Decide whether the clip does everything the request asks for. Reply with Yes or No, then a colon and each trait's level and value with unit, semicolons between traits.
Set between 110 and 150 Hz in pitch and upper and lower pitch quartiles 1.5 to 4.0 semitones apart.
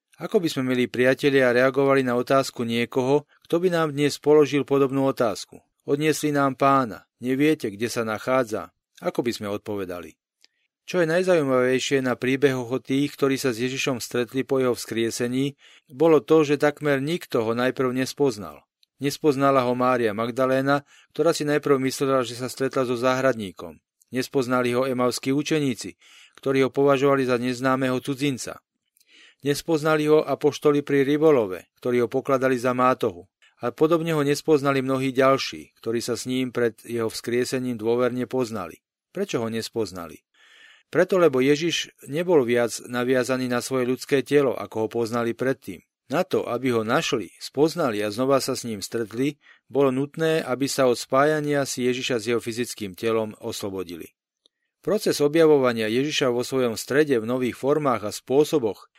Yes: low, 130 Hz; average, 2.8 semitones